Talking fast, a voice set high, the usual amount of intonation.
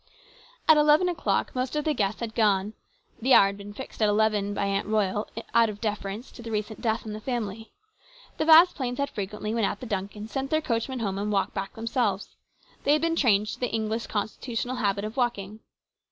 Yes: fast, 210 wpm; high, 220 Hz; average, 3.5 semitones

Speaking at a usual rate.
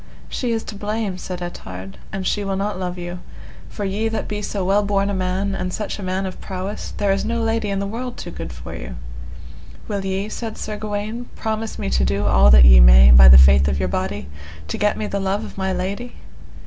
No: fast, 235 wpm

